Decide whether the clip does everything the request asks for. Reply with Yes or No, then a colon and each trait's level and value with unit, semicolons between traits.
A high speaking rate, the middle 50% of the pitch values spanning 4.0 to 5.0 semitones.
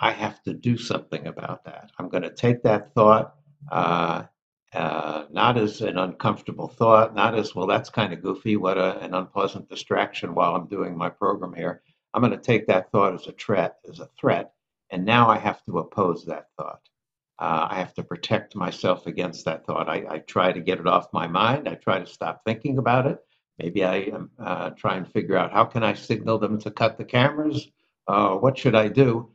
Yes: fast, 215 wpm; average, 4.3 semitones